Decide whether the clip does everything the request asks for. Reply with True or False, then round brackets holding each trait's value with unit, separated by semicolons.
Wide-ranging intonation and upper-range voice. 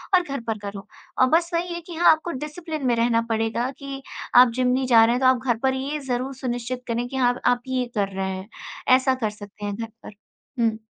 False (3.3 semitones; 250 Hz)